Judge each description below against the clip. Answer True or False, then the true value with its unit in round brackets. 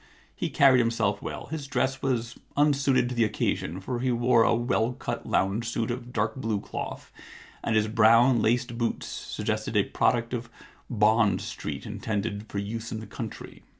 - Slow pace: False (175 wpm)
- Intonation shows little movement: True (2.3 semitones)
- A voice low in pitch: True (115 Hz)